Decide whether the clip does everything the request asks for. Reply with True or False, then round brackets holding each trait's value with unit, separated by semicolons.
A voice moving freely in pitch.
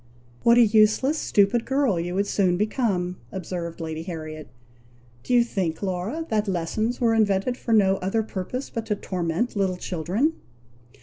False (4.4 semitones)